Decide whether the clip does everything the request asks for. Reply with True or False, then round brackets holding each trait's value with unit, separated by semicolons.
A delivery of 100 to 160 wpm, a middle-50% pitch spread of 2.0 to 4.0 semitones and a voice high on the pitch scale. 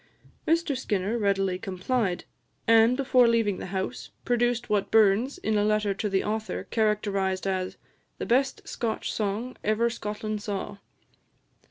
True (140 wpm; 2.9 semitones; 215 Hz)